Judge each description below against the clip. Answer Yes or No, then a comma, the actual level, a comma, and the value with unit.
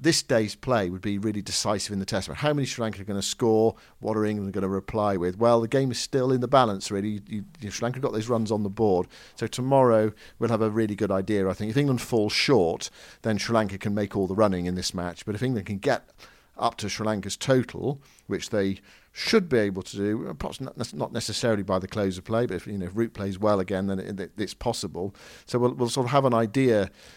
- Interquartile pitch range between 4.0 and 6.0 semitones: No, average, 3.0 semitones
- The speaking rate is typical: No, fast, 255 wpm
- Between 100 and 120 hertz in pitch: Yes, low, 110 Hz